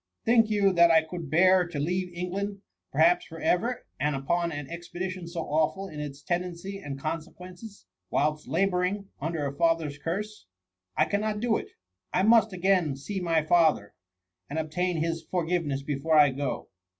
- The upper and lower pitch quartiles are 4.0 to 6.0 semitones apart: No, average, 3.6 semitones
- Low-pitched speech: No, medium, 170 Hz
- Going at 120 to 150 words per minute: No, average, 175 wpm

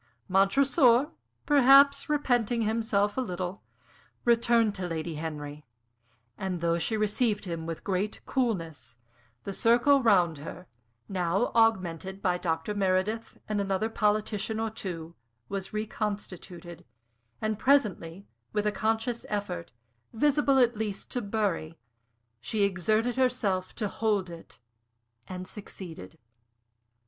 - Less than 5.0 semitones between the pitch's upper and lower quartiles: Yes, average, 4.2 semitones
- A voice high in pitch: Yes, high, 205 Hz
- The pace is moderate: No, slow, 115 wpm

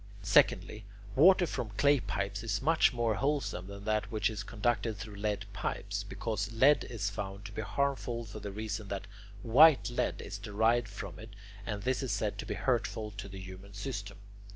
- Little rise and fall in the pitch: No, average, 3.1 semitones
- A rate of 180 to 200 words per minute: Yes, average, 185 wpm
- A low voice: Yes, low, 110 Hz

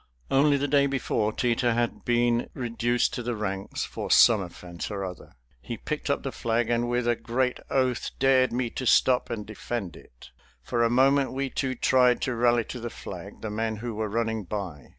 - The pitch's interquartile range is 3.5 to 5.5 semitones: No, average, 2.8 semitones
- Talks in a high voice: No, low, 120 Hz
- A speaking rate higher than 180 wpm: Yes, average, 200 wpm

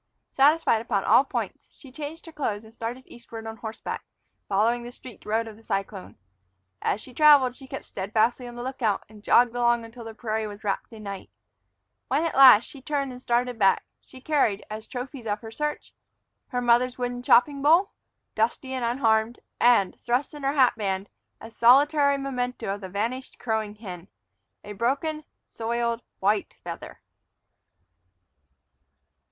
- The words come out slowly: No, average, 165 wpm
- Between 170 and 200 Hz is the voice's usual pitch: No, high, 240 Hz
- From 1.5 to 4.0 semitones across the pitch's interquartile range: Yes, average, 3.2 semitones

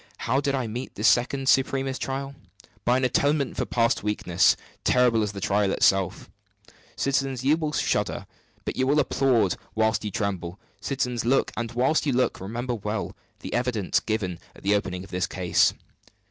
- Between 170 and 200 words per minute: Yes, average, 175 wpm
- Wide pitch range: No, average, 4.6 semitones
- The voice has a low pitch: Yes, low, 120 Hz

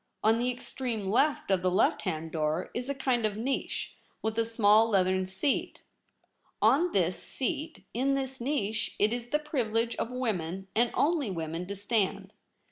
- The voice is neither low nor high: No, high, 225 Hz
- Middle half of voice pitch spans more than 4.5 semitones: Yes, average, 5.2 semitones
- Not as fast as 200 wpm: Yes, average, 175 wpm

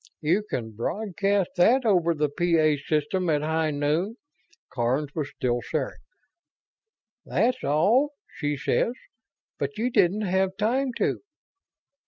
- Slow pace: Yes, slow, 130 wpm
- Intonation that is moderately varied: No, wide, 5.9 semitones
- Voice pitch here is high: No, medium, 170 Hz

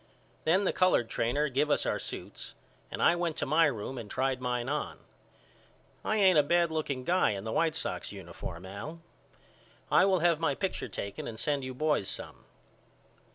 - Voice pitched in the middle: Yes, medium, 145 Hz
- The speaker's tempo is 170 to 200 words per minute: Yes, average, 185 wpm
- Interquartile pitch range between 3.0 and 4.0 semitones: No, average, 5.3 semitones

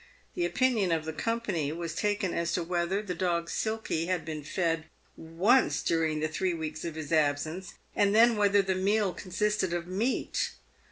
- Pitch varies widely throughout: No, average, 4.1 semitones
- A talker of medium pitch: Yes, medium, 180 Hz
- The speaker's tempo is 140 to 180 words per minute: Yes, average, 175 wpm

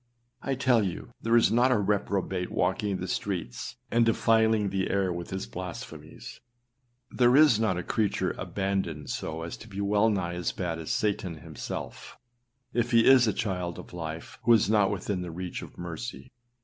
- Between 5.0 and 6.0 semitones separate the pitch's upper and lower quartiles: No, average, 4.1 semitones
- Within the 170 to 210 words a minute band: Yes, average, 185 wpm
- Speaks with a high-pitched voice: No, low, 100 Hz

